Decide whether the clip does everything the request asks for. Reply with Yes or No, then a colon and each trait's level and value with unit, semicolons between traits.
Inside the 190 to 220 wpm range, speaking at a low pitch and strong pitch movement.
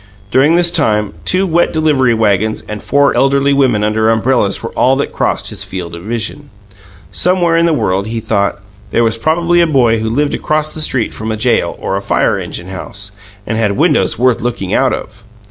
Yes: average, 200 wpm; low, 120 Hz; wide, 5.7 semitones